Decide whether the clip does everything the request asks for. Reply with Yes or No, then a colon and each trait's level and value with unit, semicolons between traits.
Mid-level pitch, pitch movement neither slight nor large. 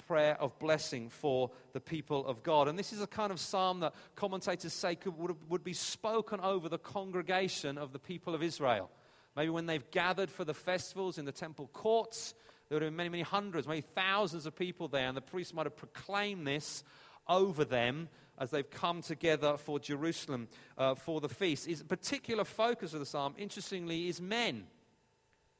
Yes: medium, 165 Hz; average, 4.2 semitones